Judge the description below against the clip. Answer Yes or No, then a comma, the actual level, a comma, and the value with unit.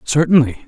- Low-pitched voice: No, medium, 145 Hz